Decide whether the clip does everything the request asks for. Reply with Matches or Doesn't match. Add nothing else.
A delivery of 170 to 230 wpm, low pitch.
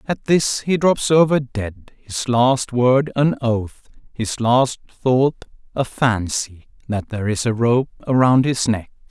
Doesn't match